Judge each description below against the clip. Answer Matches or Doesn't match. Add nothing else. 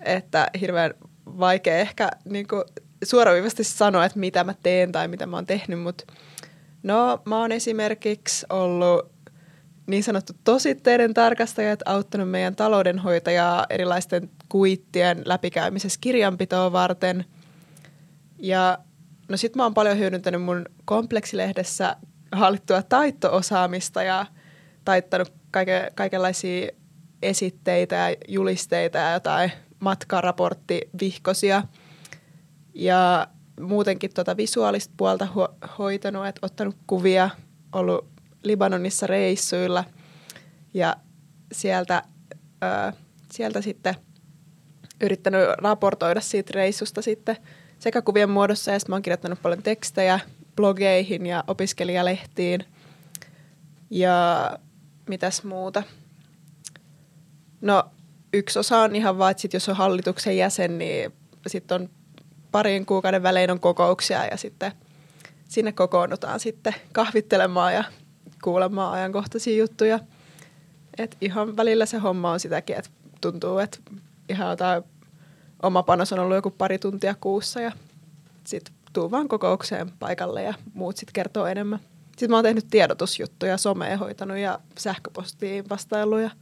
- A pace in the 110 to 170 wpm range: Matches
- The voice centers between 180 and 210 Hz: Matches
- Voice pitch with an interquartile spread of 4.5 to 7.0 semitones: Doesn't match